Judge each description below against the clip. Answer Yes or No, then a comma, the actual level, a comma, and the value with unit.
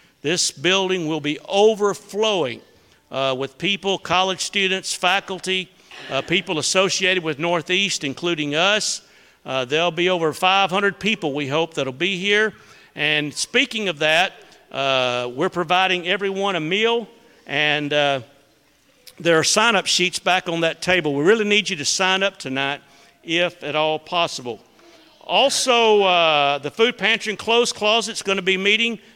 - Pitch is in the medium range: Yes, medium, 180 Hz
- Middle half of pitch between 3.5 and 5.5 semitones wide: Yes, average, 4.8 semitones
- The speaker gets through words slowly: No, average, 155 wpm